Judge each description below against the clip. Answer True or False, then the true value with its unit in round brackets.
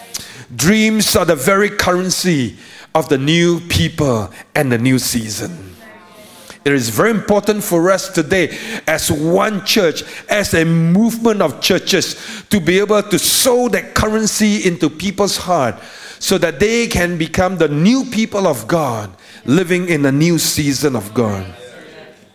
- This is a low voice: False (175 Hz)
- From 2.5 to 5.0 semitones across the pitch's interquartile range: False (5.4 semitones)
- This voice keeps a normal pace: True (150 wpm)